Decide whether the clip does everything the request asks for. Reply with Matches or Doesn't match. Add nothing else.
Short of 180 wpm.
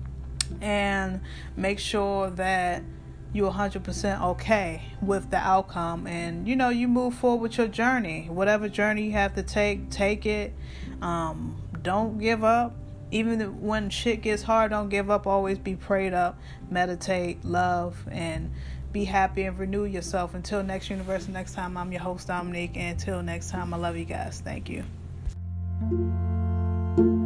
Matches